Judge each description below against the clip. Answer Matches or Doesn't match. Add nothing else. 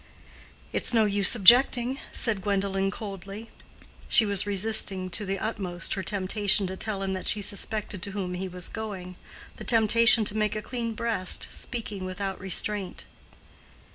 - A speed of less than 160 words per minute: Matches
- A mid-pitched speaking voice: Doesn't match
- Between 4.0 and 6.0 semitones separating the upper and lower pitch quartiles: Doesn't match